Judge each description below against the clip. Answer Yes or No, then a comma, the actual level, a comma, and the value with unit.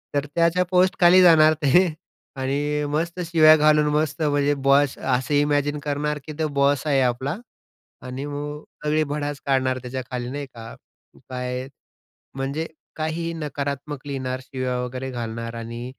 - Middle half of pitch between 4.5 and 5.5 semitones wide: No, average, 2.8 semitones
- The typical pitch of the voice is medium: Yes, medium, 145 Hz